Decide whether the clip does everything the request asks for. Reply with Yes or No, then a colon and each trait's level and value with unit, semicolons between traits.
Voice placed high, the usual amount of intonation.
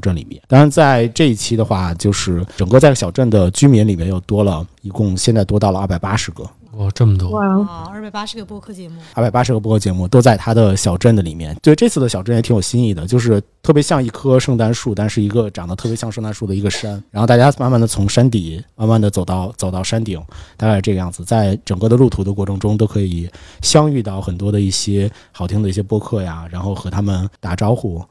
No: low, 105 Hz; average, 3.8 semitones